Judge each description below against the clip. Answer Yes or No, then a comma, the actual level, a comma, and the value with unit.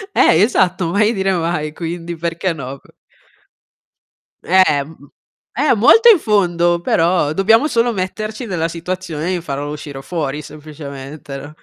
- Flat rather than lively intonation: No, average, 4.1 semitones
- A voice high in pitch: No, medium, 170 Hz